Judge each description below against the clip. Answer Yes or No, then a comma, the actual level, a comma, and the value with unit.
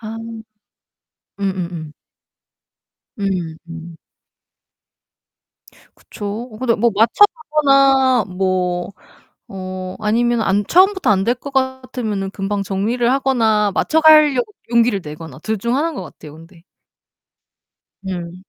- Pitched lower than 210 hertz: No, high, 215 Hz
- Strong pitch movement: Yes, wide, 5.7 semitones